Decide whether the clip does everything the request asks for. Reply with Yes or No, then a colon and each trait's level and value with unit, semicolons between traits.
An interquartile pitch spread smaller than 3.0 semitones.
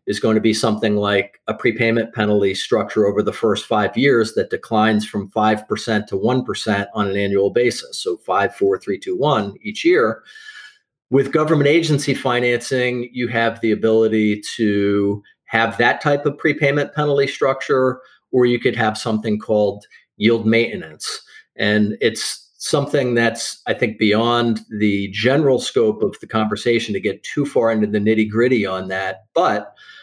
No: average, 3.7 semitones